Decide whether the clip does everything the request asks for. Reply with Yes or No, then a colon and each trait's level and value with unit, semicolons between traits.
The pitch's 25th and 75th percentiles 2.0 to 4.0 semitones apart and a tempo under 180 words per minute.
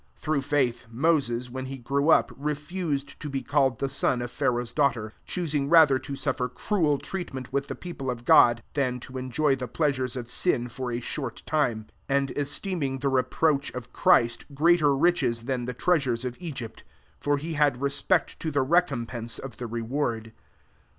No: average, 3.2 semitones; average, 185 wpm